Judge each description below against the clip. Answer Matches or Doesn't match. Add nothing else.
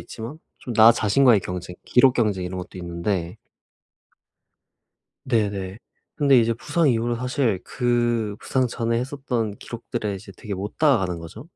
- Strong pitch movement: Doesn't match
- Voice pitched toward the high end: Doesn't match